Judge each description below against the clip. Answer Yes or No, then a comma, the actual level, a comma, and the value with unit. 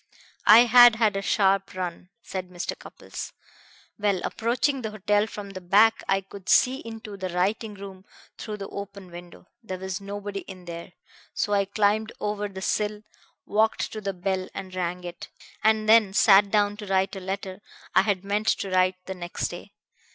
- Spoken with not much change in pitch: Yes, narrow, 2.1 semitones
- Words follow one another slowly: No, average, 180 wpm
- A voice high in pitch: Yes, high, 200 Hz